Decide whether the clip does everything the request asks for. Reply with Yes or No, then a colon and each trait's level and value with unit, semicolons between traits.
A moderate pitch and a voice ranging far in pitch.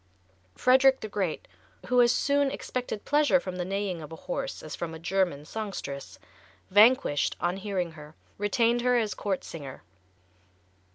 No: high, 205 Hz; wide, 6.3 semitones